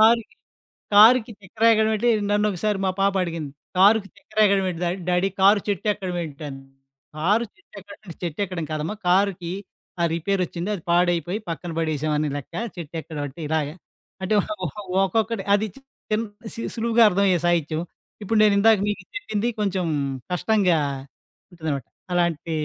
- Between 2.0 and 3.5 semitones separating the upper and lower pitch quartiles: No, average, 4.1 semitones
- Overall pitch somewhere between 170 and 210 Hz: Yes, high, 190 Hz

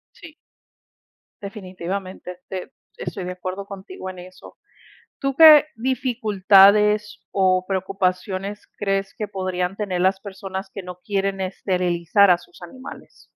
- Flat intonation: Yes, narrow, 2.0 semitones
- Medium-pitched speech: No, high, 195 Hz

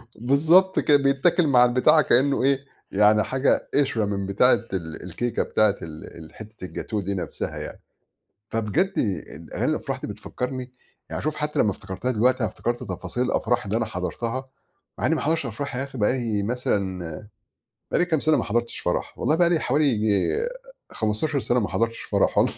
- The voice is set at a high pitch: No, low, 120 Hz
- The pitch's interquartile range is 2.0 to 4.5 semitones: No, average, 5.1 semitones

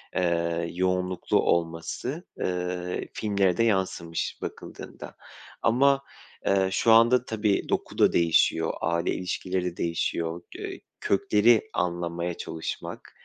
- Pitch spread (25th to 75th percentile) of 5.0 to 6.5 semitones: No, average, 3.6 semitones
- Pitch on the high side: No, very low, 90 Hz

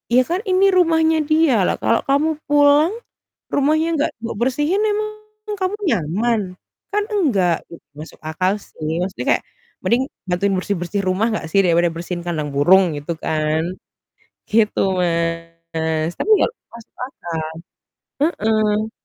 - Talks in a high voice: Yes, high, 215 Hz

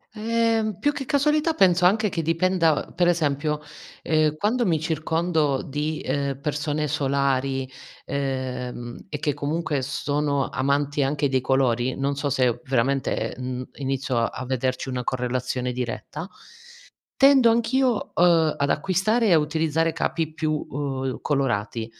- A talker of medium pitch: Yes, medium, 145 Hz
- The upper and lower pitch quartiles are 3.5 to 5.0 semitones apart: Yes, average, 4.3 semitones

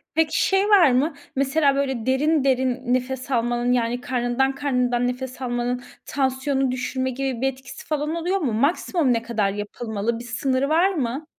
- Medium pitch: No, very high, 260 Hz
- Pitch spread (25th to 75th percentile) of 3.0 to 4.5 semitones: No, narrow, 2.5 semitones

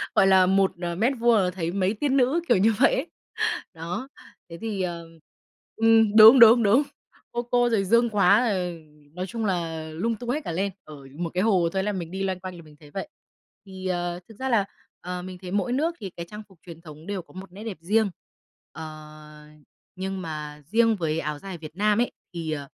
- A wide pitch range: No, average, 4.7 semitones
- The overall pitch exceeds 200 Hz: No, high, 190 Hz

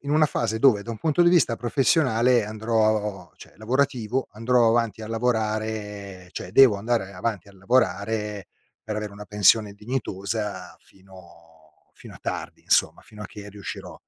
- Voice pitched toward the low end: Yes, low, 110 Hz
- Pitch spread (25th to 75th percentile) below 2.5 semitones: No, average, 2.8 semitones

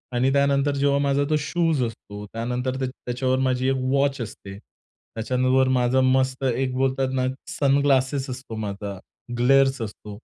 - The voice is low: Yes, low, 130 Hz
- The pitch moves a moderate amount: No, narrow, 1.9 semitones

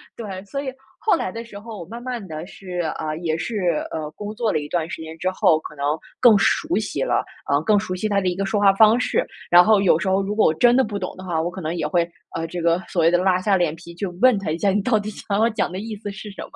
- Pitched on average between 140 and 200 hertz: Yes, high, 190 Hz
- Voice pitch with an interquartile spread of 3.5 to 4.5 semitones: Yes, average, 4.0 semitones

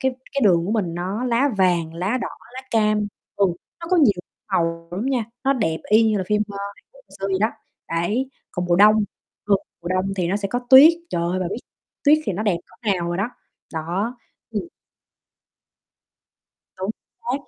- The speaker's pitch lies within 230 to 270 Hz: No, high, 200 Hz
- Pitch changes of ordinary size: Yes, average, 4.7 semitones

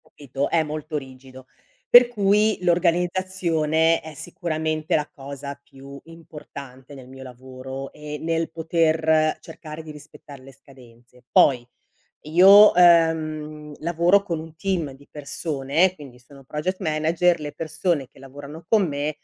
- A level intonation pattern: No, average, 3.3 semitones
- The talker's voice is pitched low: No, medium, 155 Hz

